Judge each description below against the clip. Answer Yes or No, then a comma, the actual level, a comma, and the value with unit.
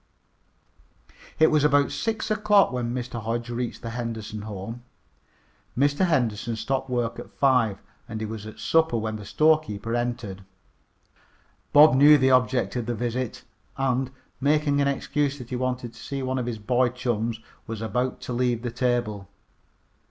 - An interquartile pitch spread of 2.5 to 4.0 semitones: Yes, average, 3.1 semitones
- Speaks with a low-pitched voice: Yes, low, 125 Hz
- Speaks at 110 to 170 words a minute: Yes, average, 160 wpm